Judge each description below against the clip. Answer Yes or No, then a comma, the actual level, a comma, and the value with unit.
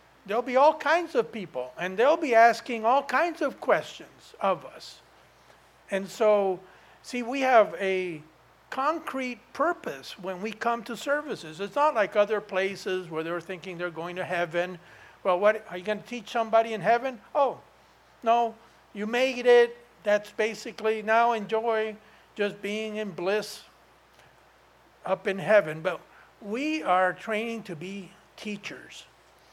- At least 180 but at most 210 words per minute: No, average, 150 wpm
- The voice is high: Yes, high, 215 Hz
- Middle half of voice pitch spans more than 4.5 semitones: No, average, 4.1 semitones